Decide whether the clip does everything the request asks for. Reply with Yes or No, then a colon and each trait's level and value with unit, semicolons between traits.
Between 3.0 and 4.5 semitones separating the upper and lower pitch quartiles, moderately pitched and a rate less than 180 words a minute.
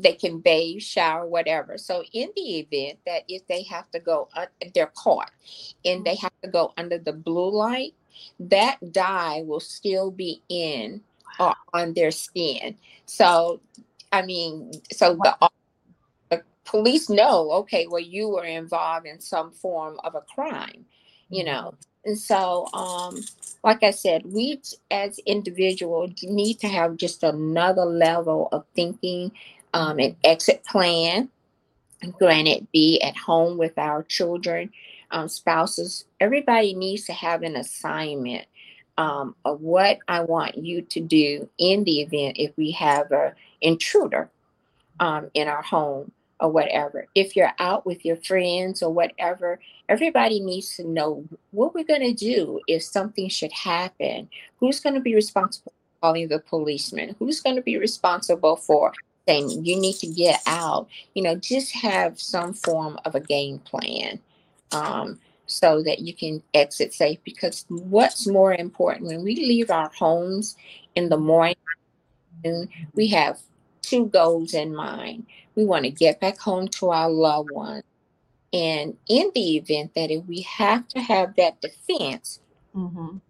Yes: average, 3.5 semitones; medium, 175 Hz; average, 155 wpm